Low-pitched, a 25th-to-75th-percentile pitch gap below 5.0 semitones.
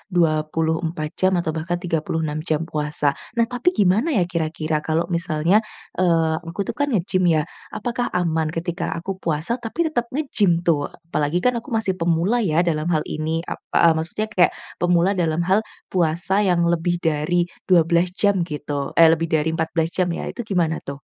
No: medium, 170 Hz; average, 2.8 semitones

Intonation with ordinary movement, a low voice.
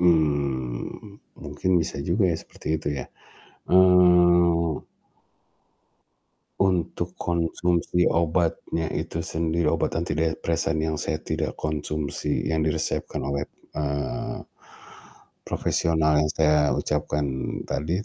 No: narrow, 2.2 semitones; very low, 80 Hz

